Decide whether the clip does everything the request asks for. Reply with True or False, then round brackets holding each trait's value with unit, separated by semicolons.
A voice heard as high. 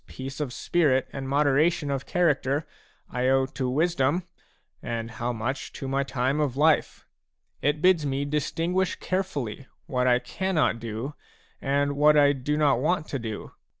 False (140 Hz)